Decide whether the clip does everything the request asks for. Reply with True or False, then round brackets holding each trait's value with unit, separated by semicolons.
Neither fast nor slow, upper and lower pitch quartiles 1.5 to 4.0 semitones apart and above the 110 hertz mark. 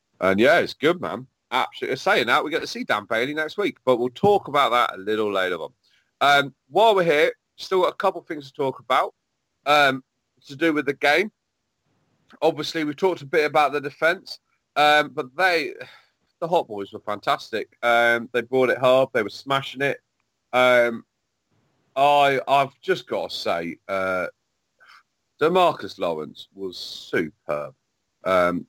False (170 wpm; 4.5 semitones; 140 Hz)